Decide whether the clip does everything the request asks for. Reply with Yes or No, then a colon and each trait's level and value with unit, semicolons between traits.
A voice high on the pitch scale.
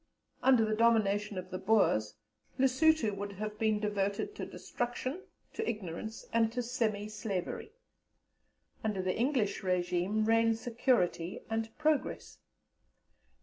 Yes: high, 215 Hz